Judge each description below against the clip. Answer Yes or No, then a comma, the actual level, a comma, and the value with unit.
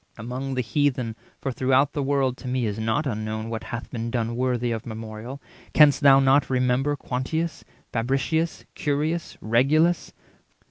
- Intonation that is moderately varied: Yes, average, 3.6 semitones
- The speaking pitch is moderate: No, low, 130 Hz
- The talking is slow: No, average, 150 wpm